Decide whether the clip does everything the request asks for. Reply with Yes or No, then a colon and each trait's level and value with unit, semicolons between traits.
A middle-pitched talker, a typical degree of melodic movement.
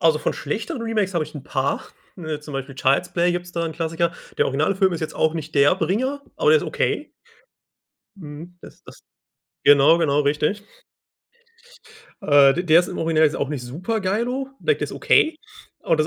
Yes: medium, 165 Hz; average, 4.4 semitones